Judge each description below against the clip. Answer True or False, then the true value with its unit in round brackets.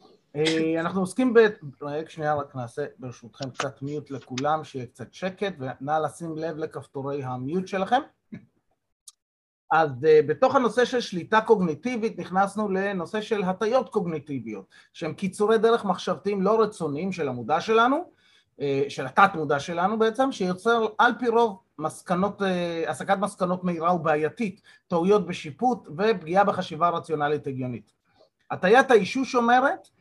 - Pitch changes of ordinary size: False (6.1 semitones)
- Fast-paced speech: False (125 wpm)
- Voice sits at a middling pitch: True (175 Hz)